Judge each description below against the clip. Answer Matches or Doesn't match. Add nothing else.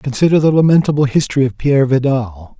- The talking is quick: Doesn't match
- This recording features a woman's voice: Doesn't match